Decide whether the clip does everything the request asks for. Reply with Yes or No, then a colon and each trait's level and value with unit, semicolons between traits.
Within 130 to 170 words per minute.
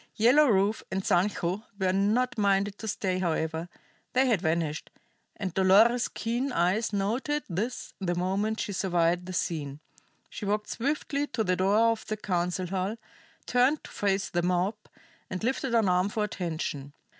Yes: average, 160 wpm